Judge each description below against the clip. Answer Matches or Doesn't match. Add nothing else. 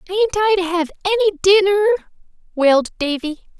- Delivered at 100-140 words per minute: Matches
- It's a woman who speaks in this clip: Matches